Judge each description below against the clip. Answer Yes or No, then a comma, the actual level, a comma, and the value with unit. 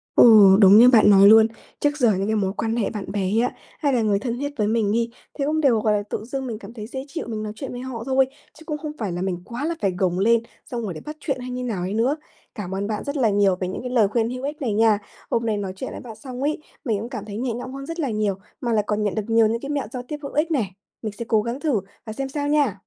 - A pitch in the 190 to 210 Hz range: No, high, 230 Hz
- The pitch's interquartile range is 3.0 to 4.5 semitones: Yes, average, 4.1 semitones